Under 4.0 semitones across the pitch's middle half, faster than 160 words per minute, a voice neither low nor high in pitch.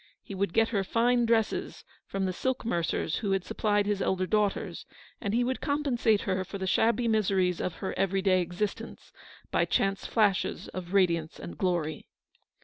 No: average, 3.3 semitones; average, 175 wpm; high, 195 Hz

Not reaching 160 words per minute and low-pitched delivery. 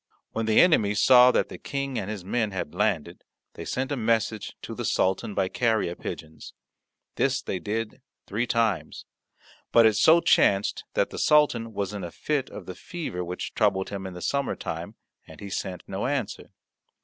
No: average, 185 wpm; low, 105 Hz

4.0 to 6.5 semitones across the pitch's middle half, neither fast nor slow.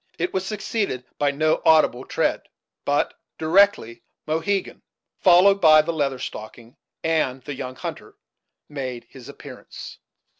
No: average, 5.2 semitones; slow, 125 wpm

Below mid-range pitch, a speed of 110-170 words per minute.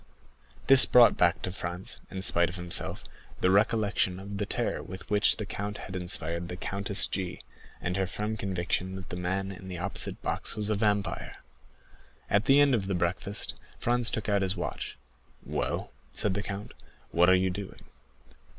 No: very low, 95 Hz; average, 180 wpm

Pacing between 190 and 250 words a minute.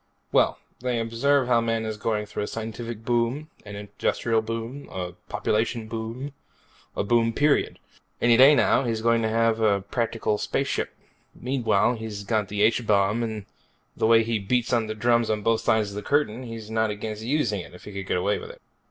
Yes: average, 195 wpm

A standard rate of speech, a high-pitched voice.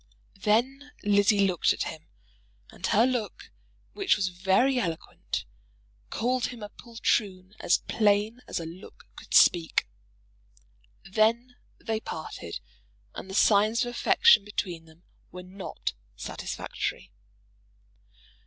No: slow, 115 wpm; high, 210 Hz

